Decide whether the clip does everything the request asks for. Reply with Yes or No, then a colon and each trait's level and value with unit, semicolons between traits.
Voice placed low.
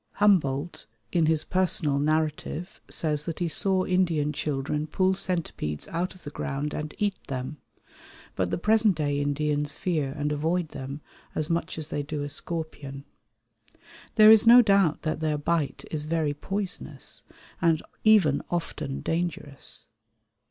No: medium, 155 Hz